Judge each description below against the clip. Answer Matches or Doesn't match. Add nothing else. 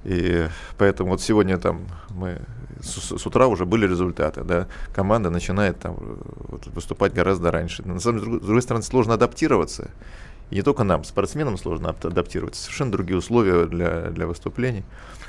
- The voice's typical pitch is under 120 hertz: Matches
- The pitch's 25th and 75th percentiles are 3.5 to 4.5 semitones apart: Matches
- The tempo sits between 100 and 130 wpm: Doesn't match